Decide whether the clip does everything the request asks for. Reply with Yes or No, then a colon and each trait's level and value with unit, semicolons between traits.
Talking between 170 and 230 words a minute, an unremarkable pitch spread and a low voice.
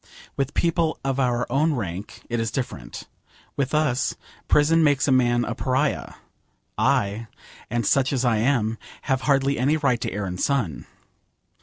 No: average, 160 wpm; average, 3.3 semitones; low, 130 Hz